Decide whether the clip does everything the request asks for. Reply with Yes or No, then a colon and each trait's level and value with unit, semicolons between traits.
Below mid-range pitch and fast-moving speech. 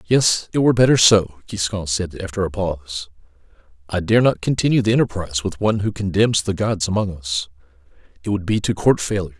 No: very low, 95 Hz; average, 190 wpm